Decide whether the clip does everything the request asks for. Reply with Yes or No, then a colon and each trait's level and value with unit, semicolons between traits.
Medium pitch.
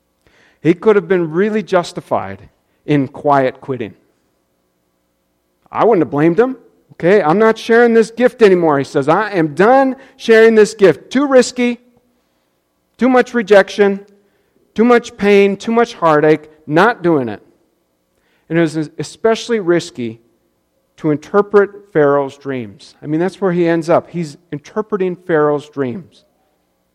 Yes: medium, 165 Hz